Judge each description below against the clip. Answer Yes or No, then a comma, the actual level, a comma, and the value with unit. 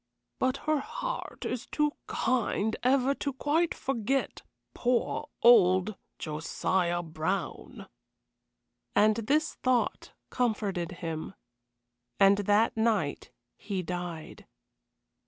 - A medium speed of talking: No, slow, 95 wpm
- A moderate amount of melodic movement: No, wide, 6.1 semitones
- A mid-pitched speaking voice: No, high, 220 Hz